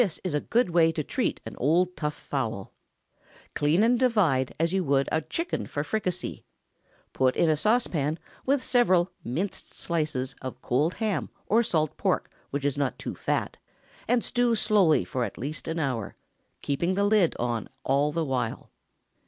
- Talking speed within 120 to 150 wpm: No, average, 170 wpm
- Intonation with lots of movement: Yes, wide, 6.3 semitones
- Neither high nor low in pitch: Yes, medium, 160 Hz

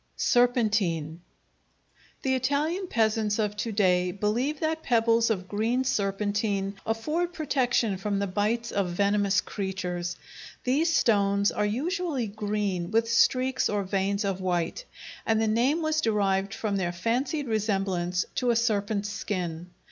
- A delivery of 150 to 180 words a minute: No, slow, 135 wpm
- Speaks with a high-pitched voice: Yes, high, 210 Hz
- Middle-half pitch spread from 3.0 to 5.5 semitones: Yes, average, 3.7 semitones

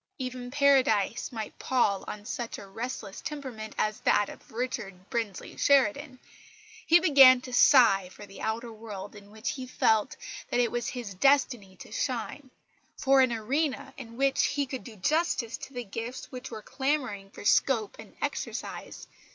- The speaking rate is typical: Yes, average, 165 wpm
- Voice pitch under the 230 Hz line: No, high, 240 Hz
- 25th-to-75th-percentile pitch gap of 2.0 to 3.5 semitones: No, average, 3.9 semitones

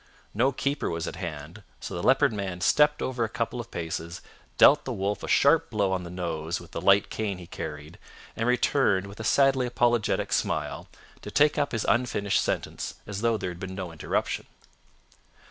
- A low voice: Yes, low, 100 Hz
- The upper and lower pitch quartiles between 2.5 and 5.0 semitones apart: No, wide, 5.5 semitones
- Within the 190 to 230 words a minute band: Yes, average, 195 wpm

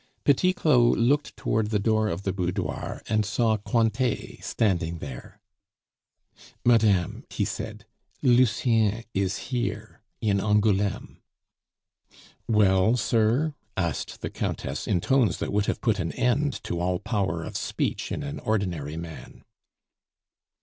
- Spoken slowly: Yes, slow, 130 wpm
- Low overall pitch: Yes, low, 110 Hz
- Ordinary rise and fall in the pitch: Yes, average, 3.9 semitones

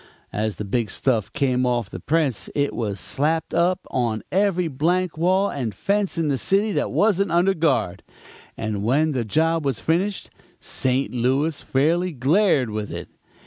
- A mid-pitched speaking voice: Yes, medium, 145 Hz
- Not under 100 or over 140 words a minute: No, average, 165 wpm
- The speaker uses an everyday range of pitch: No, wide, 6.4 semitones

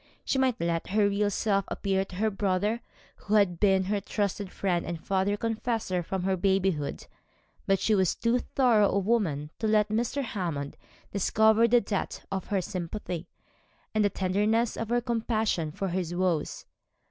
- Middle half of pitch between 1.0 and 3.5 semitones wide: Yes, average, 3.0 semitones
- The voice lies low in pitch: No, high, 200 Hz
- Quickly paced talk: No, average, 165 wpm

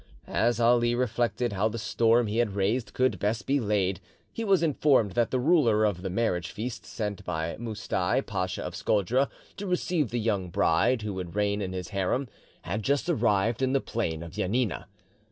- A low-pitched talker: Yes, low, 110 Hz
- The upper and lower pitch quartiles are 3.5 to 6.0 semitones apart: Yes, average, 4.0 semitones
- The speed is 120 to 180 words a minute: No, average, 190 wpm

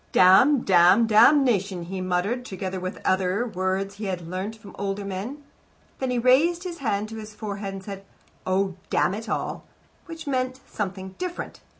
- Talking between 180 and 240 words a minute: Yes, average, 185 wpm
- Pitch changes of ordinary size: Yes, average, 4.7 semitones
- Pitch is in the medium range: No, high, 200 Hz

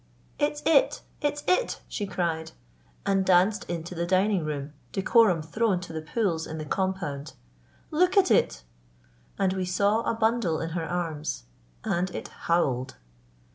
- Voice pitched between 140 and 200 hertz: Yes, medium, 185 Hz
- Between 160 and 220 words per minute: No, average, 150 wpm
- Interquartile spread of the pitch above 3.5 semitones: Yes, average, 5.2 semitones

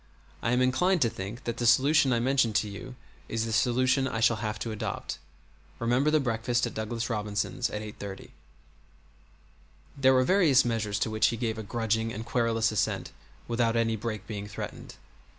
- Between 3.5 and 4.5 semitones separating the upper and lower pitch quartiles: No, narrow, 2.5 semitones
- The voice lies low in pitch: Yes, low, 115 Hz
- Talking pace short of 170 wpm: No, average, 180 wpm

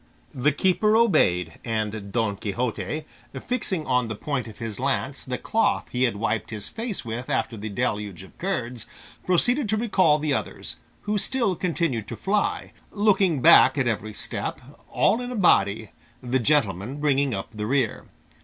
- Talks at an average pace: Yes, average, 165 wpm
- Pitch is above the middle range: No, low, 130 Hz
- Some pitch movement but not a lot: No, wide, 8.8 semitones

